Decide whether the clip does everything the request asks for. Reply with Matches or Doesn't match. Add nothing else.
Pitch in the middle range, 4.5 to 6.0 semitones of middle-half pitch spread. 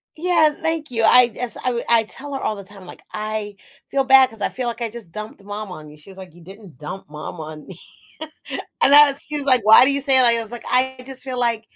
Doesn't match